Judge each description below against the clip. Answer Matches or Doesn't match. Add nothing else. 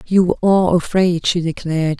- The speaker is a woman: Matches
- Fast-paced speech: Doesn't match